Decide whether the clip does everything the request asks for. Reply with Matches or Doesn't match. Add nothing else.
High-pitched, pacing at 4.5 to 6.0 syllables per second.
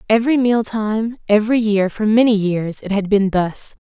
Matches